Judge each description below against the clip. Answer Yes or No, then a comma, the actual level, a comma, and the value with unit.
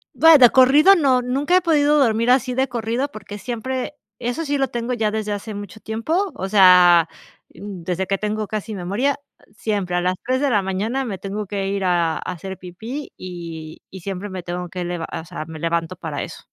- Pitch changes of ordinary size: No, wide, 5.9 semitones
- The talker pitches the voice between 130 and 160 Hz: No, high, 210 Hz